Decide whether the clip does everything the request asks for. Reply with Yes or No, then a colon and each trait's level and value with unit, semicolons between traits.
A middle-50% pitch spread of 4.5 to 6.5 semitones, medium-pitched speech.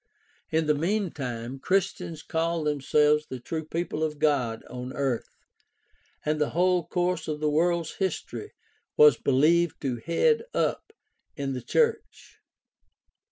No: average, 3.5 semitones; medium, 155 Hz